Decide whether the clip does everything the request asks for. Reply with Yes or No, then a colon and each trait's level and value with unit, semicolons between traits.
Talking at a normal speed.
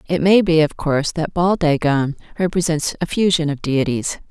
Yes: average, 180 wpm